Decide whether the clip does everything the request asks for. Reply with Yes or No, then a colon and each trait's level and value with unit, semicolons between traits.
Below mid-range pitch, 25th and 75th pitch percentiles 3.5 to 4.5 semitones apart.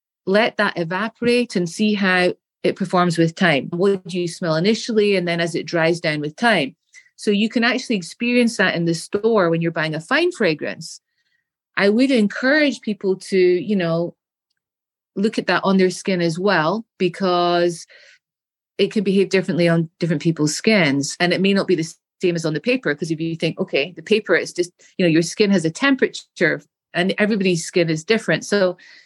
No: medium, 185 Hz; average, 4.0 semitones